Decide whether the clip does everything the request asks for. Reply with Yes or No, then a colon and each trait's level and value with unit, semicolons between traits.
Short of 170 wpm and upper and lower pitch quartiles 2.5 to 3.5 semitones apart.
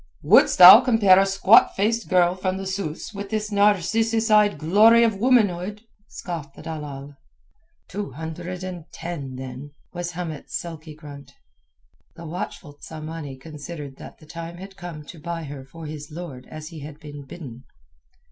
No: average, 160 wpm; average, 4.5 semitones